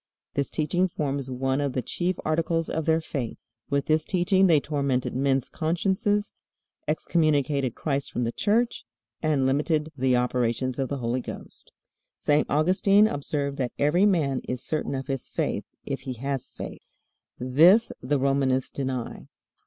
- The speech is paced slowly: No, average, 155 wpm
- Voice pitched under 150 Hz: Yes, medium, 140 Hz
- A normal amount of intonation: Yes, average, 3.6 semitones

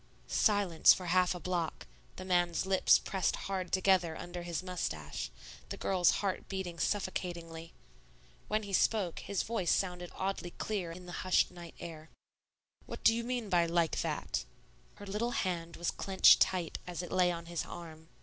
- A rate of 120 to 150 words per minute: No, average, 170 wpm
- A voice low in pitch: No, medium, 180 Hz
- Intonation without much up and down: Yes, narrow, 2.1 semitones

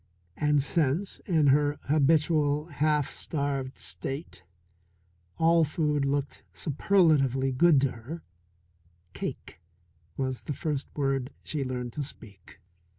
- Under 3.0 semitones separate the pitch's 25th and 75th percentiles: Yes, narrow, 2.5 semitones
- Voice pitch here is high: No, medium, 145 Hz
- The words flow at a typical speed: No, slow, 110 wpm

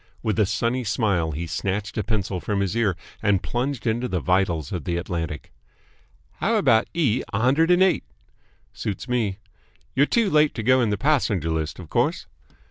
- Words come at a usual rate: Yes, average, 190 wpm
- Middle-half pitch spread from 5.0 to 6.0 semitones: Yes, wide, 5.6 semitones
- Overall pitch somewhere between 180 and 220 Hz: No, low, 105 Hz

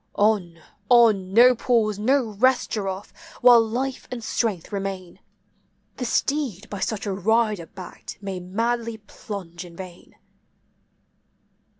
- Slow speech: Yes, slow, 120 wpm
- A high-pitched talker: Yes, high, 210 Hz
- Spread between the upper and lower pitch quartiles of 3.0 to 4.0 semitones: Yes, average, 3.7 semitones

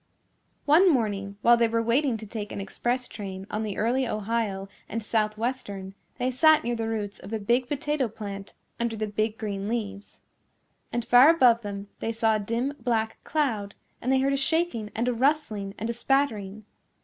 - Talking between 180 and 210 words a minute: Yes, average, 185 wpm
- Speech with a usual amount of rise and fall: Yes, average, 3.3 semitones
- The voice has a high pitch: Yes, high, 225 Hz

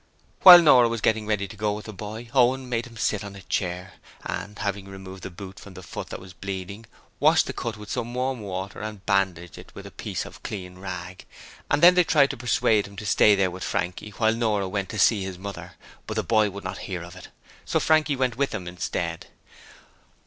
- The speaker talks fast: Yes, fast, 230 wpm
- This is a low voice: Yes, low, 105 Hz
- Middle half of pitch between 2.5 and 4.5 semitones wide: Yes, average, 3.4 semitones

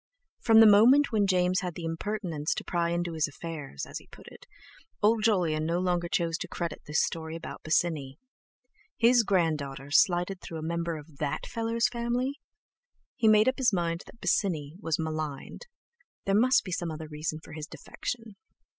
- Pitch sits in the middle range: Yes, medium, 175 Hz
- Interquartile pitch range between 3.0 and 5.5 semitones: Yes, average, 5.2 semitones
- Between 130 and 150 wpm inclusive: No, average, 175 wpm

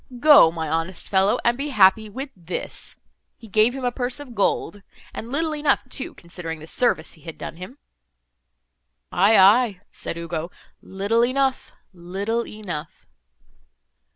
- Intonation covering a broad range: Yes, wide, 6.1 semitones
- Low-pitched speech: No, high, 205 Hz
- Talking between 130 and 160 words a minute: Yes, average, 140 wpm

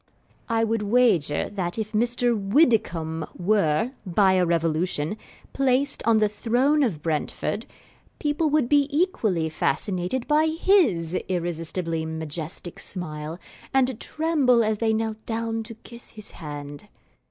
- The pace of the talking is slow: Yes, slow, 130 wpm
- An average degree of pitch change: No, wide, 6.7 semitones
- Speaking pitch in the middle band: No, high, 215 Hz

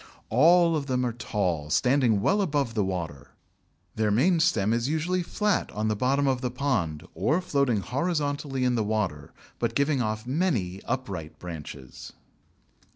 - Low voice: Yes, low, 125 Hz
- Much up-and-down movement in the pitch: Yes, wide, 5.8 semitones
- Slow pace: No, average, 155 wpm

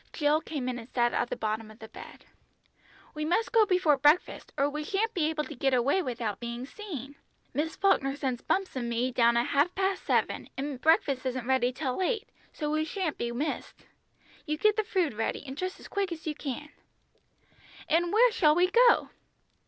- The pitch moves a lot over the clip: Yes, wide, 6.2 semitones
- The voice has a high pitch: Yes, very high, 295 Hz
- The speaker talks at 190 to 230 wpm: Yes, average, 200 wpm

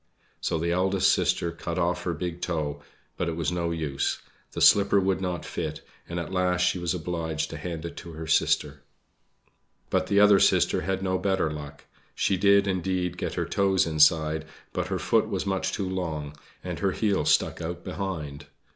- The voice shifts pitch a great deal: No, average, 2.9 semitones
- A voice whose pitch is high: No, very low, 85 Hz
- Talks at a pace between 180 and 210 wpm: Yes, average, 190 wpm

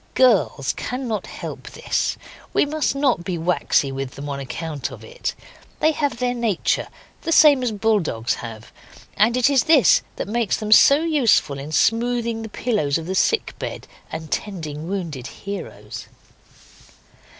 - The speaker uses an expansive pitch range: Yes, wide, 8.3 semitones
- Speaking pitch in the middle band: No, high, 215 Hz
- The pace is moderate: Yes, average, 160 wpm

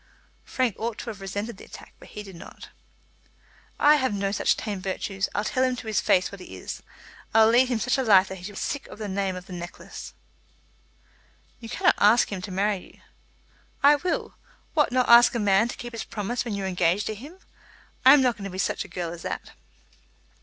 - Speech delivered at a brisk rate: Yes, fast, 230 wpm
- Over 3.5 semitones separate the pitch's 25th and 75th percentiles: Yes, average, 3.9 semitones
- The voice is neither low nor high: No, high, 210 Hz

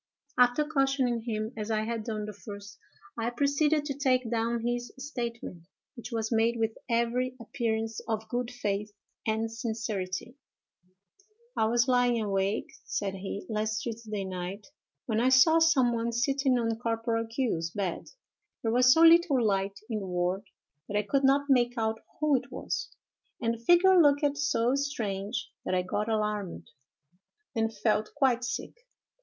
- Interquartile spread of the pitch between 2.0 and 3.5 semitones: Yes, average, 3.1 semitones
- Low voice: No, high, 230 Hz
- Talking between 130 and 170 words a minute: Yes, average, 160 wpm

